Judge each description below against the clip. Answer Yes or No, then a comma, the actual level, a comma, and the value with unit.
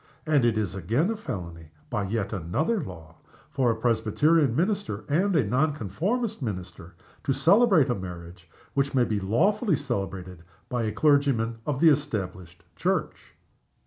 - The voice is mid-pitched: No, low, 115 Hz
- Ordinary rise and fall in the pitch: No, wide, 8.0 semitones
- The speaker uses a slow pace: No, average, 145 wpm